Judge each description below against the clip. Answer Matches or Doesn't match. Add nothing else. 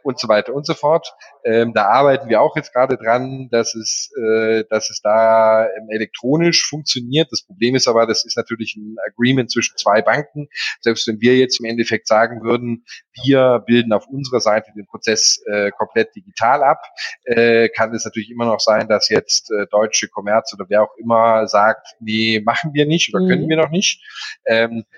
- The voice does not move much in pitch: Doesn't match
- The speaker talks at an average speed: Doesn't match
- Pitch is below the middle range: Matches